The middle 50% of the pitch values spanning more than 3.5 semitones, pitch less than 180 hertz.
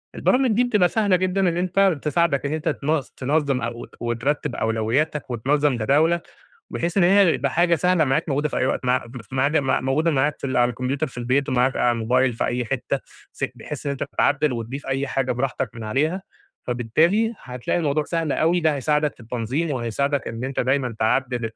Yes: average, 4.3 semitones; medium, 140 Hz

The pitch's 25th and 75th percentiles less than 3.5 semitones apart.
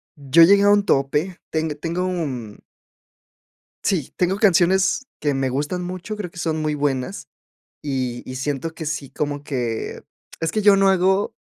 No: average, 5.1 semitones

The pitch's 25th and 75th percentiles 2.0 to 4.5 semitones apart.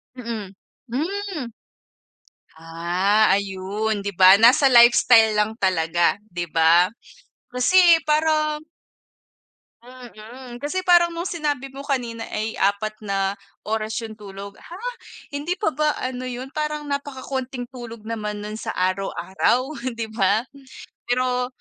No: average, 5.2 semitones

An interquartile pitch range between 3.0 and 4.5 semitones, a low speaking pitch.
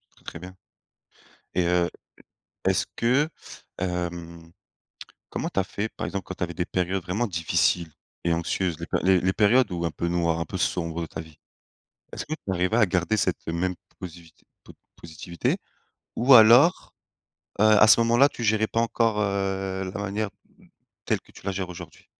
Yes: average, 3.6 semitones; very low, 95 Hz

